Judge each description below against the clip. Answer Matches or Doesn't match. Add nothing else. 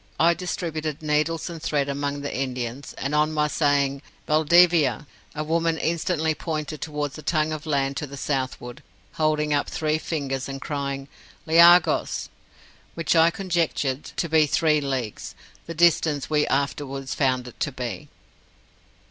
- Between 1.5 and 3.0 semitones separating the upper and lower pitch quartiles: Matches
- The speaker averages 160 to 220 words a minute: Doesn't match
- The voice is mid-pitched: Matches